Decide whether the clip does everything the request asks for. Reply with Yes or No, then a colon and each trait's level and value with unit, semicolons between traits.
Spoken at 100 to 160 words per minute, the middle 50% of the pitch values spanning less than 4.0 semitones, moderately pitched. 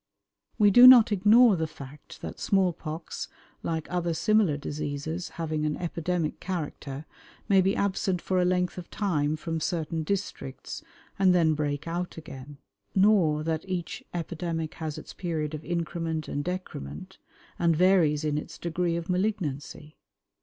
Yes: average, 150 wpm; average, 3.1 semitones; medium, 165 Hz